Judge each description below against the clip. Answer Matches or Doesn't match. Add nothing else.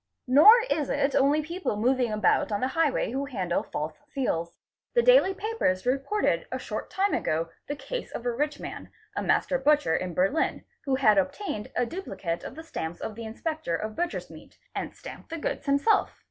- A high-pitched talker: Matches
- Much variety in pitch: Matches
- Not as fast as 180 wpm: Doesn't match